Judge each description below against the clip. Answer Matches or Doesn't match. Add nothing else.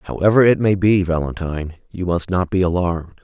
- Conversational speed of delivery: Matches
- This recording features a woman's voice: Doesn't match